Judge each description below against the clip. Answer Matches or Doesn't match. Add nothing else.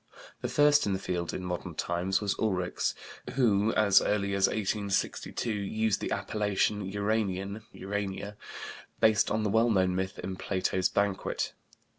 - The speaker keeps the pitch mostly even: Matches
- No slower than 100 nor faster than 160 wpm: Matches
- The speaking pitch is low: Matches